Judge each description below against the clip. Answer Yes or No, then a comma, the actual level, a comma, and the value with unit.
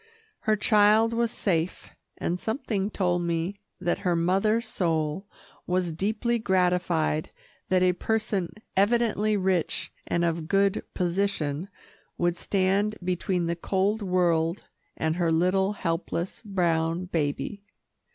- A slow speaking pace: Yes, slow, 120 wpm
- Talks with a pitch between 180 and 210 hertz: Yes, medium, 185 Hz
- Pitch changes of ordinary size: Yes, average, 3.1 semitones